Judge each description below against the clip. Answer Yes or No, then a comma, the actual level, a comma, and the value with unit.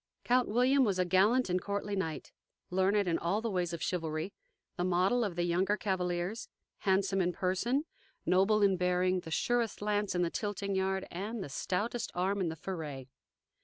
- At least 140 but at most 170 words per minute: No, average, 180 wpm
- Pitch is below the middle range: No, high, 190 Hz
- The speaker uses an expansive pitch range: No, narrow, 2.6 semitones